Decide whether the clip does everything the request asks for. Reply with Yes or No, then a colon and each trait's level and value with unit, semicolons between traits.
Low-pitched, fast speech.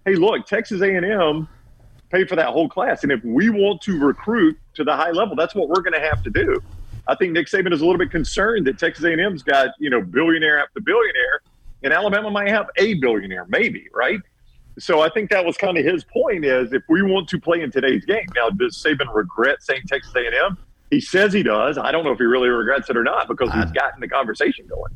No: high, 205 Hz; fast, 235 wpm